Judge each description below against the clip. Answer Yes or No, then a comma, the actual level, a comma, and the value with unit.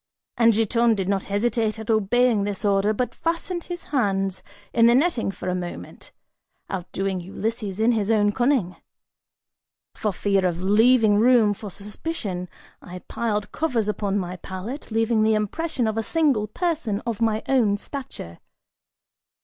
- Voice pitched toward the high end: Yes, high, 215 Hz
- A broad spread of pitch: No, average, 3.4 semitones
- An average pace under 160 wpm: Yes, average, 150 wpm